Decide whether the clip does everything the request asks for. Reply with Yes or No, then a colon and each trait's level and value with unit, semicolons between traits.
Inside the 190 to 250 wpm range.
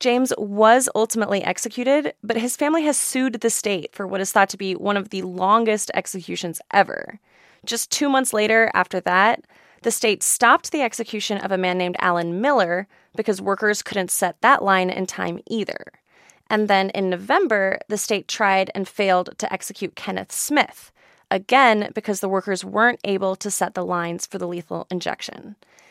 No: average, 175 wpm